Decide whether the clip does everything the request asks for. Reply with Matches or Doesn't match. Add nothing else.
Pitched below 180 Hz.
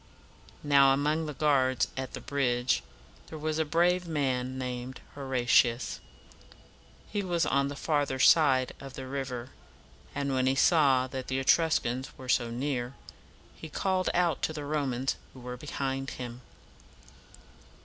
Matches